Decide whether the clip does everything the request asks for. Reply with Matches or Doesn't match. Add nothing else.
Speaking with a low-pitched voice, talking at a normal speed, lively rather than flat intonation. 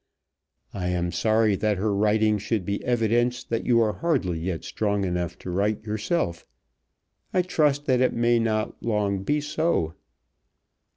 Doesn't match